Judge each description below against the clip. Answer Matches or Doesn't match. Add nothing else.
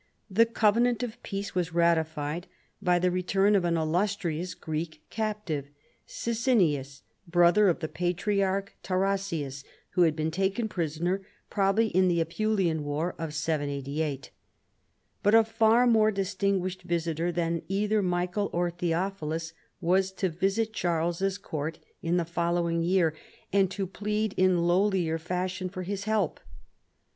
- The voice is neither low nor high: Matches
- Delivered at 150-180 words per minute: Doesn't match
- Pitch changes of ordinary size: Matches